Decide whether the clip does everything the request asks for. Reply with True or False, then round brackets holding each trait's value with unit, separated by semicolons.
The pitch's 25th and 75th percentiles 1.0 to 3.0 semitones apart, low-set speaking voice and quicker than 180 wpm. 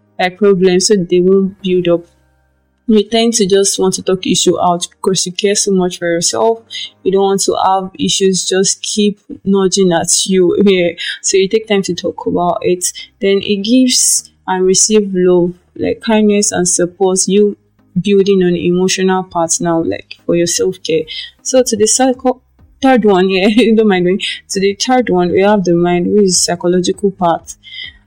False (2.7 semitones; 190 Hz; 190 wpm)